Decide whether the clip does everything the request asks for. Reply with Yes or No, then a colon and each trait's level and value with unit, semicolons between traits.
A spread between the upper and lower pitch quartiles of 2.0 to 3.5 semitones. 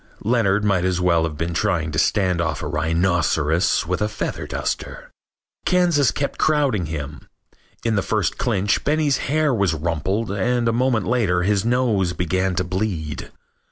No: wide, 5.4 semitones